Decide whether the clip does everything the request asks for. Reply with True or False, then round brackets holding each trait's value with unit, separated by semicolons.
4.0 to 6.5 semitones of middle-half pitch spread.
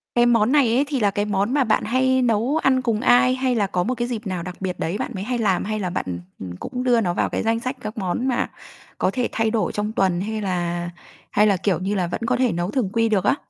True (4.5 semitones)